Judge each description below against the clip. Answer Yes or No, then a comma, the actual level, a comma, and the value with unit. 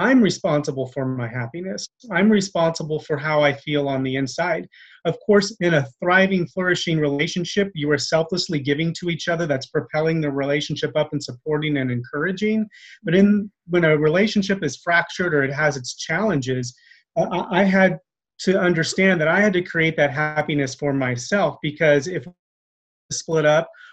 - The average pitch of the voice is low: No, medium, 160 Hz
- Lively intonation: No, average, 4.0 semitones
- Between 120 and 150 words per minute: No, average, 170 wpm